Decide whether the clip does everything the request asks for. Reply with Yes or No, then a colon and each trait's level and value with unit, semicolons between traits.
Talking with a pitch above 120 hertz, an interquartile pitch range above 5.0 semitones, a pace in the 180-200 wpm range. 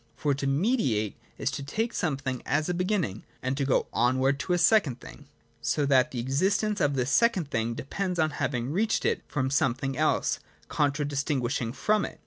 Yes: medium, 140 Hz; wide, 5.4 semitones; average, 195 wpm